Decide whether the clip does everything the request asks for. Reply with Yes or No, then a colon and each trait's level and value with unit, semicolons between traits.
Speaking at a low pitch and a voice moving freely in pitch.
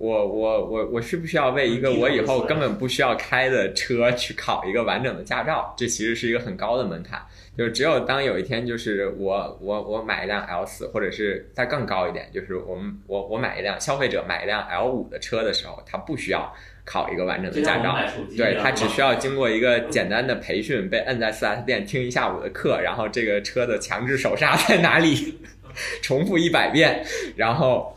Yes: low, 120 Hz; wide, 6.6 semitones